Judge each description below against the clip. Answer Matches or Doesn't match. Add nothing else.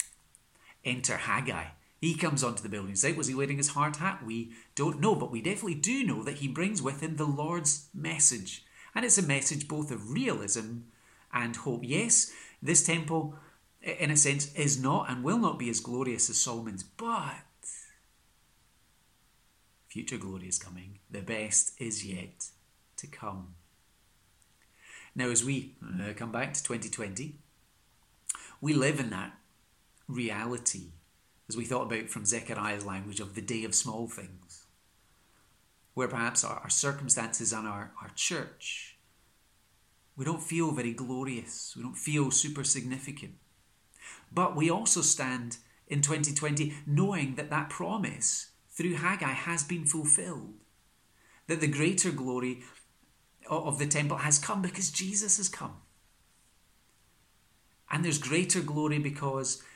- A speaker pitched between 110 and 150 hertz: Matches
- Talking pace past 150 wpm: Doesn't match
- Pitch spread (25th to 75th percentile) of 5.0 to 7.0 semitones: Matches